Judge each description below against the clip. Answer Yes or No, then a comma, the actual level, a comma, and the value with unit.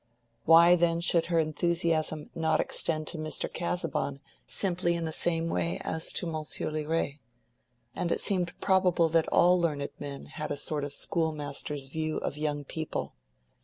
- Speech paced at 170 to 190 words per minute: No, average, 160 wpm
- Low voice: No, medium, 160 Hz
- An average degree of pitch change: No, narrow, 2.1 semitones